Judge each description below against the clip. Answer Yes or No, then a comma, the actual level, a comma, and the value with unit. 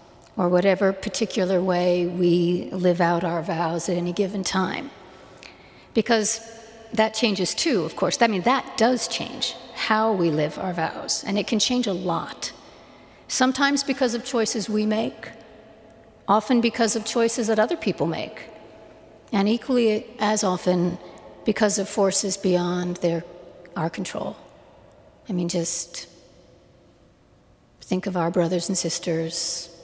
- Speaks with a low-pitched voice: No, high, 195 Hz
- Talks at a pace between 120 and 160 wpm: Yes, average, 140 wpm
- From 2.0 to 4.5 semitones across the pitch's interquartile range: Yes, average, 4.1 semitones